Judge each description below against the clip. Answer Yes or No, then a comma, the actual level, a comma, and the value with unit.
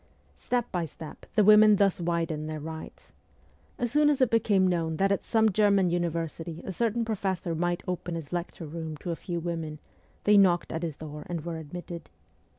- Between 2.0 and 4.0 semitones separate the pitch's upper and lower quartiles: Yes, average, 3.6 semitones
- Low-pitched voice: No, medium, 175 Hz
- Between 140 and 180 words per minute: No, average, 190 wpm